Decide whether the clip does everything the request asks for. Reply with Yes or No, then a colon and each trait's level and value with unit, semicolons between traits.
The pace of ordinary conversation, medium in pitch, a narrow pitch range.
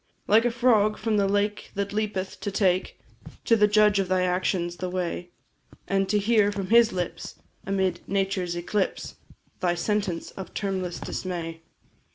No: average, 160 wpm; high, 195 Hz; narrow, 2.3 semitones